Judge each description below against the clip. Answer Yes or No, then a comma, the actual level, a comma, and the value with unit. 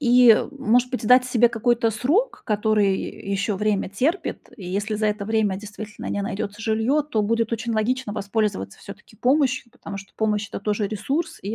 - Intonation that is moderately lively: Yes, average, 3.1 semitones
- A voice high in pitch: Yes, high, 220 Hz